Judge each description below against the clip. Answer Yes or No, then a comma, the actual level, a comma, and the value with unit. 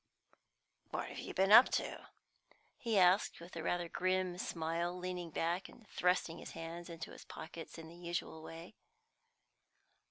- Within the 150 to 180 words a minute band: Yes, average, 155 wpm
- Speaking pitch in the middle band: Yes, medium, 175 Hz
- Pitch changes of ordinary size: No, narrow, 1.7 semitones